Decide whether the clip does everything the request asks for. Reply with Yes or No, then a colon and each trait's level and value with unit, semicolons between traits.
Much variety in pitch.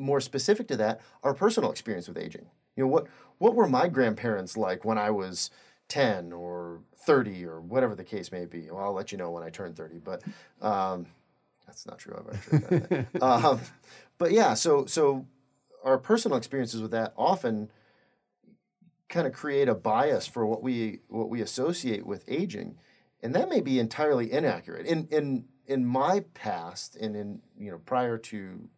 Yes: wide, 6.6 semitones